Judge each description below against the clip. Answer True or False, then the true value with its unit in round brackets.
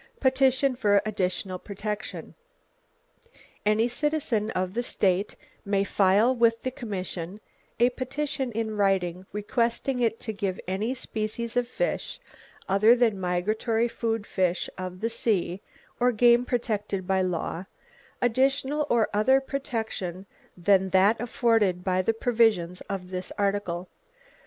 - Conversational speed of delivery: False (130 wpm)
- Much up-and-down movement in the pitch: False (4.1 semitones)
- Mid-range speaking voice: False (215 Hz)